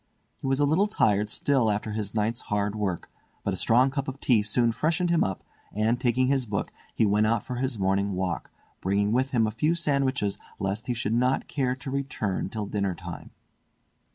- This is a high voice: No, low, 115 Hz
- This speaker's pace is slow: No, fast, 205 wpm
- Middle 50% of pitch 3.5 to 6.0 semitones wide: Yes, average, 4.4 semitones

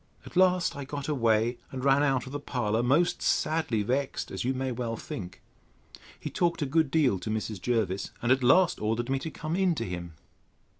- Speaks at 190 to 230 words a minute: Yes, fast, 205 wpm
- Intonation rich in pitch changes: No, average, 4.7 semitones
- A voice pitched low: Yes, low, 130 Hz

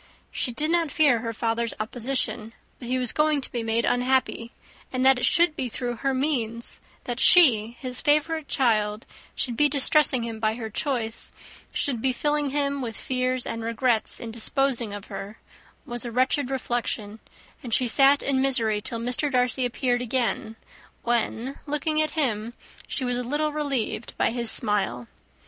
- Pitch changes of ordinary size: Yes, average, 3.3 semitones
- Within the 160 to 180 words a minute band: Yes, average, 170 wpm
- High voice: Yes, very high, 250 Hz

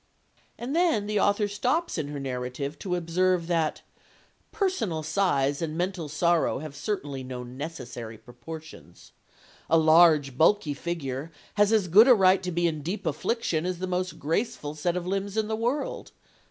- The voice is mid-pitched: Yes, medium, 170 Hz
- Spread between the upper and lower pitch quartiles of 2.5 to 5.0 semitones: No, wide, 5.4 semitones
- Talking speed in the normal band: Yes, average, 165 wpm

